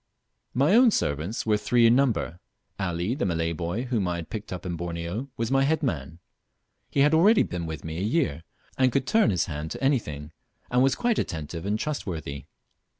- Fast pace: No, average, 195 wpm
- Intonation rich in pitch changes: Yes, wide, 8.1 semitones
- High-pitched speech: No, low, 100 Hz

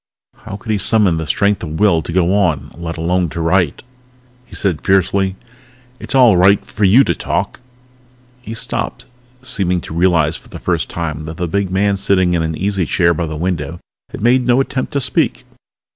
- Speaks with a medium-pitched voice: No, very low, 95 Hz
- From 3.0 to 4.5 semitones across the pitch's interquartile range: Yes, average, 3.7 semitones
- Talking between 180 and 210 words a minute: Yes, average, 200 wpm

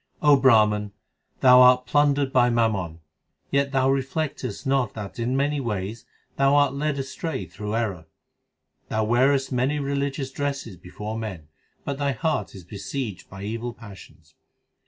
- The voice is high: No, low, 125 Hz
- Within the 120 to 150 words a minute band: Yes, average, 145 wpm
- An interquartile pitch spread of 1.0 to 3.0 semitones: No, average, 4.7 semitones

